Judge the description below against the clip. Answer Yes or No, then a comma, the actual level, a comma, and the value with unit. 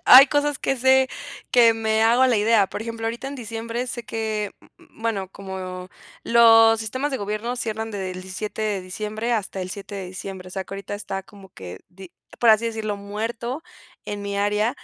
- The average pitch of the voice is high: Yes, high, 220 Hz